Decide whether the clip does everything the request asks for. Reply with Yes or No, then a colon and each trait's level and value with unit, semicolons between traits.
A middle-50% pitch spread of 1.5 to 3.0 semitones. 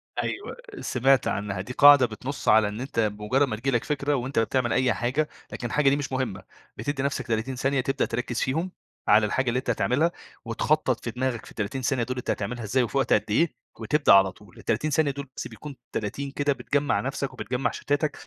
No: average, 3.6 semitones